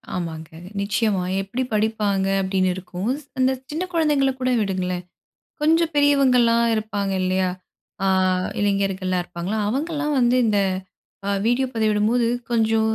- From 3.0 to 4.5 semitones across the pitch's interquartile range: No, average, 5.0 semitones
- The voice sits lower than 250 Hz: Yes, high, 215 Hz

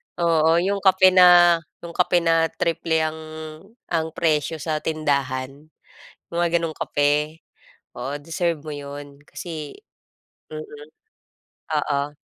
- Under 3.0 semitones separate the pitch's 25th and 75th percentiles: Yes, narrow, 2.5 semitones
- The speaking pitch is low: No, medium, 160 Hz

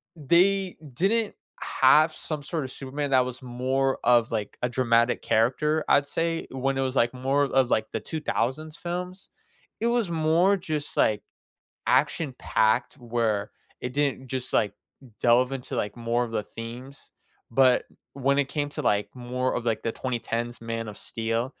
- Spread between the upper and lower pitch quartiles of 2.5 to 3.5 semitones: No, average, 4.2 semitones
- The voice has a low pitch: Yes, low, 130 Hz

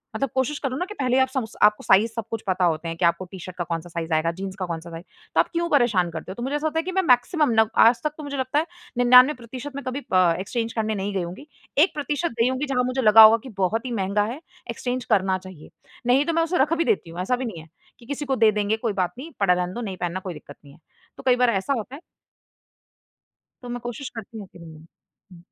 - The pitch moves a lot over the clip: Yes, wide, 6.2 semitones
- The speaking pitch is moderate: No, high, 225 Hz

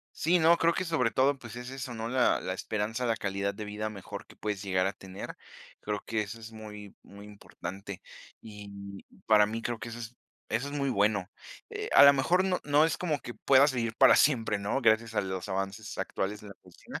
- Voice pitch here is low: Yes, low, 110 Hz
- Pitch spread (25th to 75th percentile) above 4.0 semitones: Yes, average, 4.4 semitones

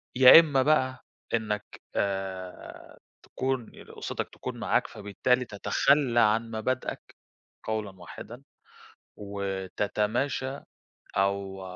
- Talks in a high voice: No, low, 110 Hz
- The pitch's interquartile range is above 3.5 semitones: Yes, average, 4.6 semitones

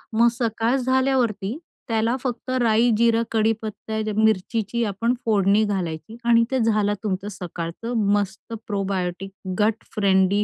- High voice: Yes, high, 220 Hz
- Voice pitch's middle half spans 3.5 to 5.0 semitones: No, average, 2.8 semitones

